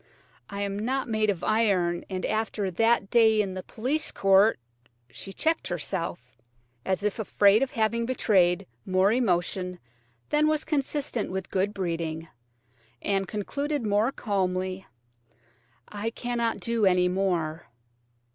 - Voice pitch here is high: Yes, high, 200 Hz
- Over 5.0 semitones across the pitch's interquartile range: No, average, 3.8 semitones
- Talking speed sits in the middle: No, slow, 130 wpm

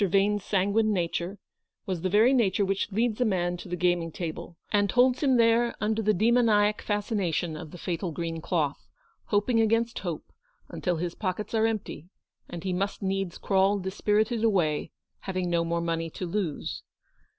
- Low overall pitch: No, high, 195 Hz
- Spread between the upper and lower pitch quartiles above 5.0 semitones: No, average, 3.7 semitones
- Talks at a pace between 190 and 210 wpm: No, average, 170 wpm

